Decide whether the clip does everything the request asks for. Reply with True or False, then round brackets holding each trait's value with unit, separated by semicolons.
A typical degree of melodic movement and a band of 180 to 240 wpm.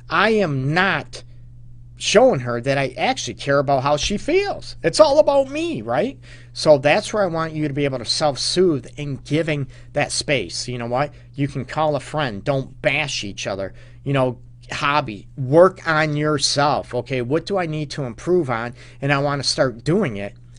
True (4.0 semitones; 190 wpm)